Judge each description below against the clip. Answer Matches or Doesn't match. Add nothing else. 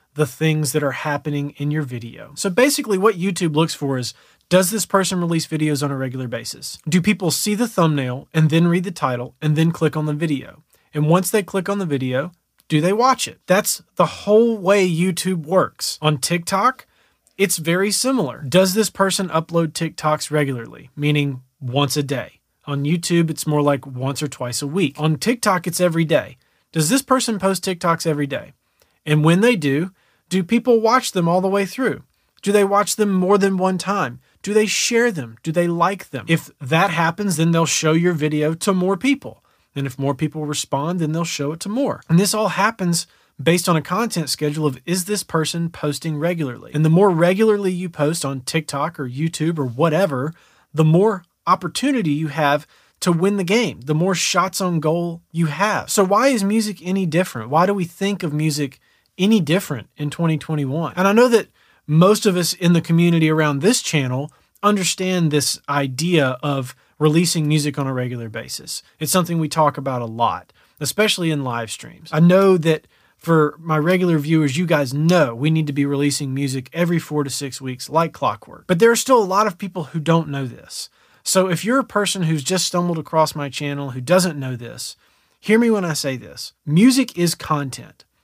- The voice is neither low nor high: Matches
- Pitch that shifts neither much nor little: Matches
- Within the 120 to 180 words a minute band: Doesn't match